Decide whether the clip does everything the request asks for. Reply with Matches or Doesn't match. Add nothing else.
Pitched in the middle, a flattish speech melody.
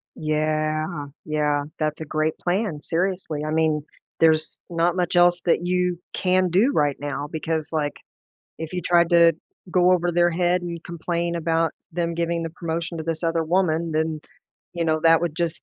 Matches